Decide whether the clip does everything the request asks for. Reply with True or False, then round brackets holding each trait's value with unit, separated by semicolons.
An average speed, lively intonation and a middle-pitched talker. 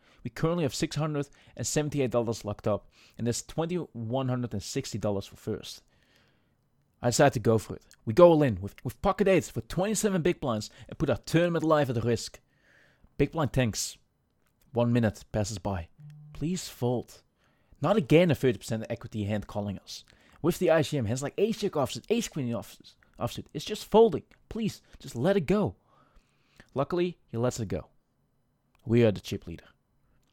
False (160 wpm; 6.3 semitones; 125 Hz)